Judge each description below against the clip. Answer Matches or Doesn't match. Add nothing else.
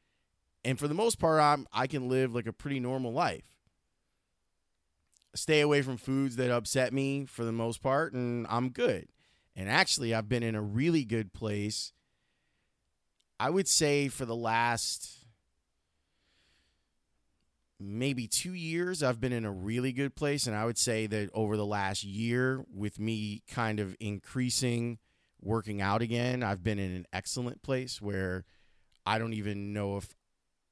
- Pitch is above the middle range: Doesn't match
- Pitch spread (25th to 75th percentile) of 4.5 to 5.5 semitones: Matches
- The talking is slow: Doesn't match